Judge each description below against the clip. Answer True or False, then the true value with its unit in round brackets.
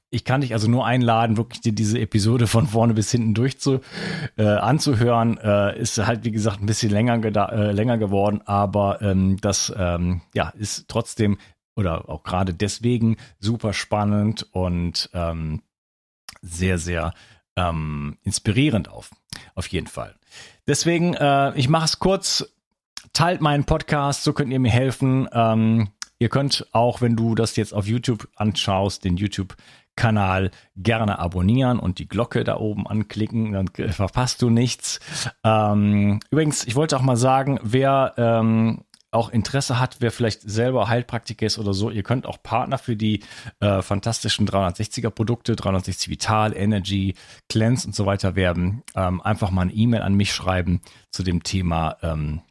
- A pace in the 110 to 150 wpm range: False (160 wpm)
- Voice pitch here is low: True (110 Hz)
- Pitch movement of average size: True (3.4 semitones)